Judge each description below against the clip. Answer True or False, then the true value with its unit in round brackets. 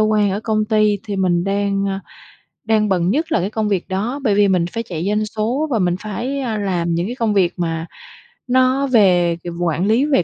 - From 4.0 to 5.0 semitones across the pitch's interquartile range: False (3.4 semitones)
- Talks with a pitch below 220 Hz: True (205 Hz)